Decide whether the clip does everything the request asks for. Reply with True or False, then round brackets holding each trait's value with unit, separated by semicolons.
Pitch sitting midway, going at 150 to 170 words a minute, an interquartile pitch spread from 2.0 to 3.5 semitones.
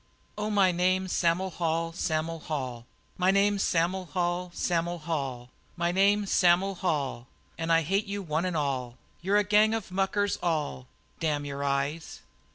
False (175 Hz; 165 wpm; 3.9 semitones)